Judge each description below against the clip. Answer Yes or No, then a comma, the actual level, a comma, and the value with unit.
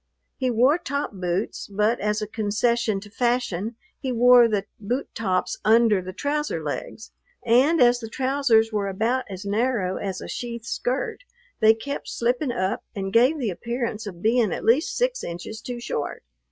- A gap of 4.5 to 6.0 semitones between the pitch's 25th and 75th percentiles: No, average, 3.6 semitones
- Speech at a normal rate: Yes, average, 170 wpm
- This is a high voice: Yes, high, 230 Hz